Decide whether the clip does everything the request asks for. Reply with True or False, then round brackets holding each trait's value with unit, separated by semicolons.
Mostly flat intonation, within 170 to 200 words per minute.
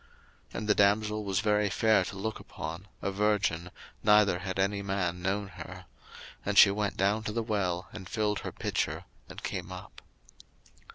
True (1.7 semitones; 175 wpm)